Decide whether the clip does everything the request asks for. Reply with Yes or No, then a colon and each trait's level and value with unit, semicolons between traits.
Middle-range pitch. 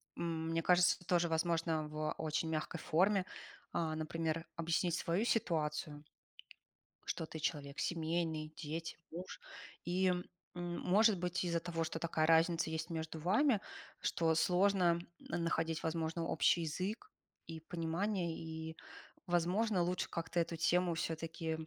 Yes: medium, 165 Hz